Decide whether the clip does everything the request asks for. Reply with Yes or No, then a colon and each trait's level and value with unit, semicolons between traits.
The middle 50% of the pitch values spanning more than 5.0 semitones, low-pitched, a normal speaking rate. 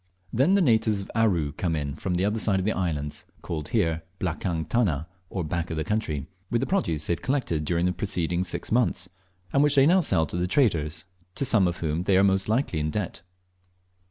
No: wide, 5.4 semitones; very low, 90 Hz; fast, 220 wpm